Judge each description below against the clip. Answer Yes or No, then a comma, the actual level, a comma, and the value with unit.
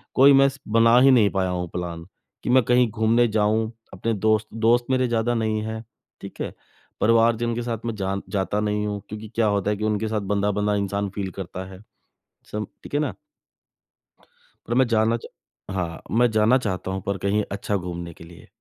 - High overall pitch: No, low, 110 Hz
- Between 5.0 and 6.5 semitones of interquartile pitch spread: No, average, 2.7 semitones